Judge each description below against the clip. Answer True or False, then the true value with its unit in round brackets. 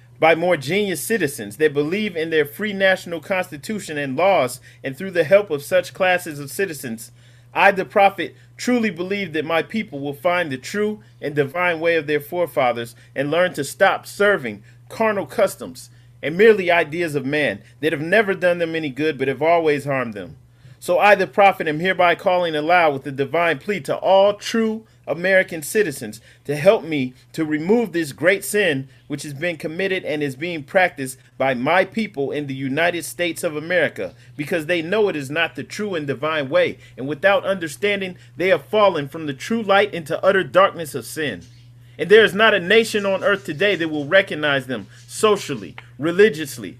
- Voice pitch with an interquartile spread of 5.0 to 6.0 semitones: True (5.5 semitones)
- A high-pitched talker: False (165 Hz)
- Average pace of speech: True (190 wpm)